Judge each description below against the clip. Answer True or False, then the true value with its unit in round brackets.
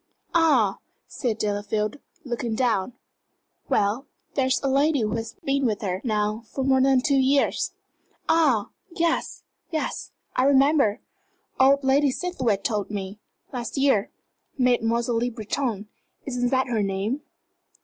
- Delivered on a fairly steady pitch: False (4.2 semitones)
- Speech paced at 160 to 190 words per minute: False (140 wpm)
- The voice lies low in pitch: False (245 Hz)